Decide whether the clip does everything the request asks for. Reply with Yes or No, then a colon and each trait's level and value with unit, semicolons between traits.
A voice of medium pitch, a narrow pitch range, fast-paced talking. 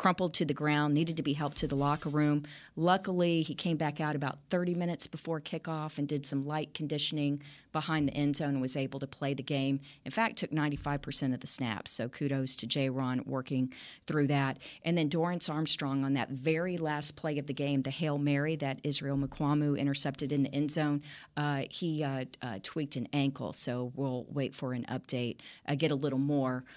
Yes: medium, 145 Hz; narrow, 2.1 semitones; fast, 215 wpm